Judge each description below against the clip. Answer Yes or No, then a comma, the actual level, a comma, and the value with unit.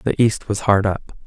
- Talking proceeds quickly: Yes, fast, 240 wpm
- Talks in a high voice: No, low, 105 Hz